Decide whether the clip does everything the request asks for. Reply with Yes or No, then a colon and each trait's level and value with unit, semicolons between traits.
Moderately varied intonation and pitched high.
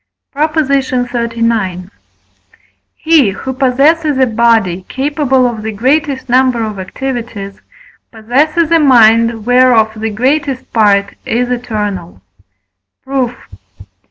Yes: average, 3.5 semitones; high, 245 Hz